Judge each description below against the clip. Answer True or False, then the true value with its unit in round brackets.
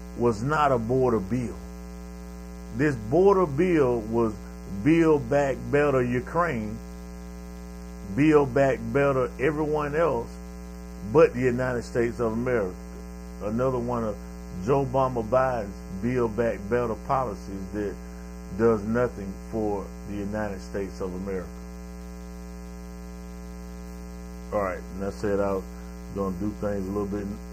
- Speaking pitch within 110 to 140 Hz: False (100 Hz)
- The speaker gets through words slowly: True (120 wpm)